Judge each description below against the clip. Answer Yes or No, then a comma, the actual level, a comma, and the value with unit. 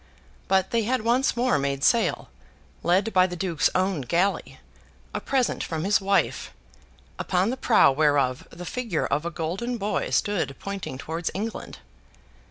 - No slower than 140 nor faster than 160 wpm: Yes, average, 155 wpm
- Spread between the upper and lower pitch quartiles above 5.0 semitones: Yes, wide, 5.5 semitones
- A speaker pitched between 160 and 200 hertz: Yes, high, 190 Hz